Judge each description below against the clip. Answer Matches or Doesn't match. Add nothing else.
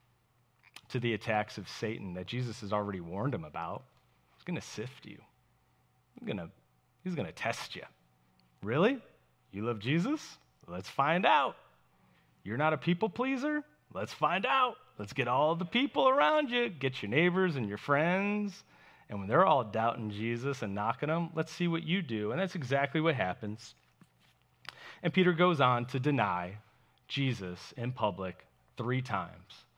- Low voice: Matches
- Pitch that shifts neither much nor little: Doesn't match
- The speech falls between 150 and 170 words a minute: Matches